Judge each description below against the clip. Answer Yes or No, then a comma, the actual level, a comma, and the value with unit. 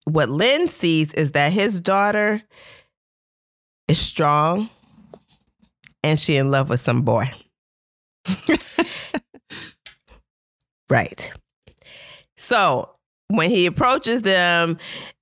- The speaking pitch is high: No, medium, 175 Hz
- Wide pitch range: Yes, wide, 6.2 semitones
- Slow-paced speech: Yes, slow, 85 wpm